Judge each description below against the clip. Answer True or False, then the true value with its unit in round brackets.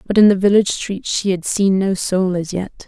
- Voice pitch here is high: True (195 Hz)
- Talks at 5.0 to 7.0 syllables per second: True (5.2 syllables/s)